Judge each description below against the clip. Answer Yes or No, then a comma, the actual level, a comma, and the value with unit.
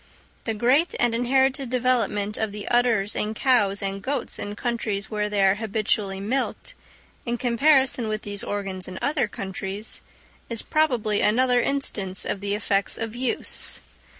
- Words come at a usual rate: Yes, average, 150 wpm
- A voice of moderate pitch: No, high, 220 Hz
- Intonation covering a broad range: No, average, 3.6 semitones